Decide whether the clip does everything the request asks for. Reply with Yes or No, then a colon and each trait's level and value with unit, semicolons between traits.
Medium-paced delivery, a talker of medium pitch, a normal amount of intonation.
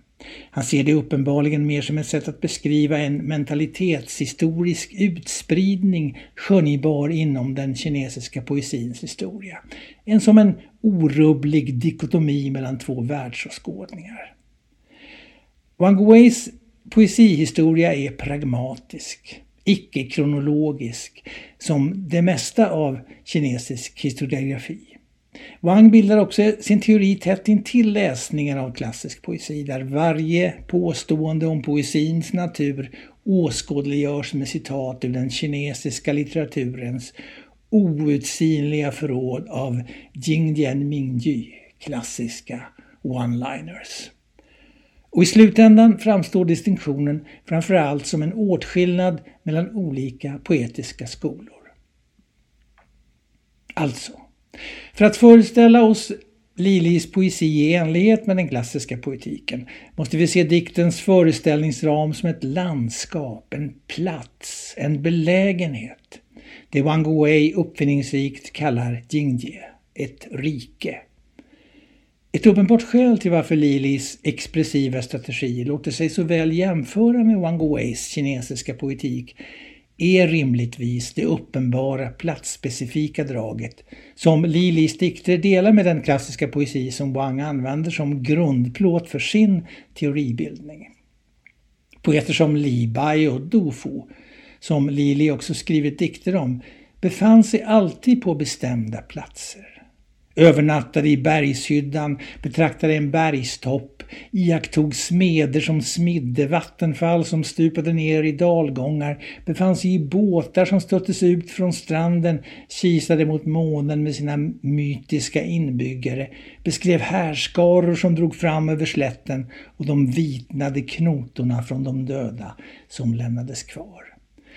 No: slow, 110 wpm; medium, 155 Hz; average, 4.3 semitones